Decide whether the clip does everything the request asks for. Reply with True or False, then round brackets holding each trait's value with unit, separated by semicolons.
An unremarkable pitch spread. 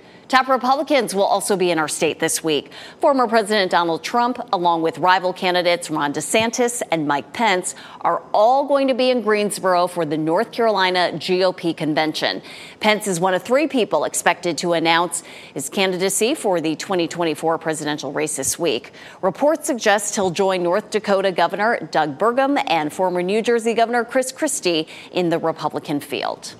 False (5.7 semitones)